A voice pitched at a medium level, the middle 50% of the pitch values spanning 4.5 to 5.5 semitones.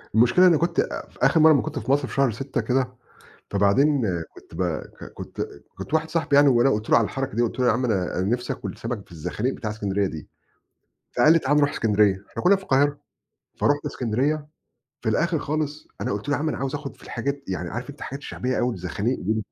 No: low, 130 Hz; average, 5.0 semitones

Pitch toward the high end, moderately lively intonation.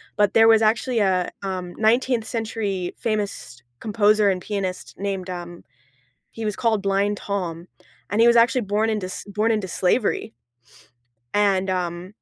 Yes: high, 205 Hz; average, 3.0 semitones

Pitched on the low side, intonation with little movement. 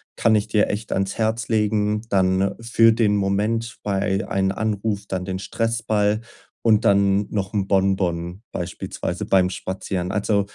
Yes: low, 100 Hz; narrow, 2.1 semitones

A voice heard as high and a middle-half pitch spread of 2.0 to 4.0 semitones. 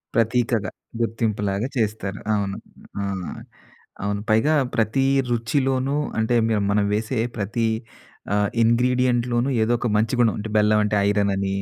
No: low, 110 Hz; average, 2.7 semitones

